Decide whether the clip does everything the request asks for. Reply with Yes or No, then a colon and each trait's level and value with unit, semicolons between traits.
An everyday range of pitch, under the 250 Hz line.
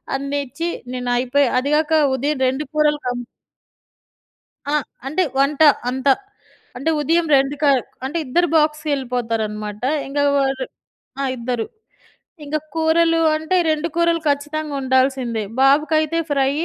No: average, 3.1 semitones; very high, 285 Hz